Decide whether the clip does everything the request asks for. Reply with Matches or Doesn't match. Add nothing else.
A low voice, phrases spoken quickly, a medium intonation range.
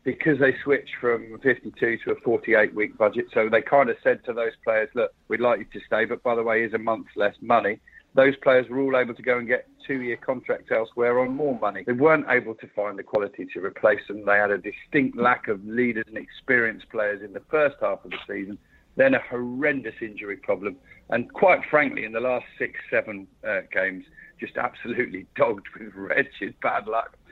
Matches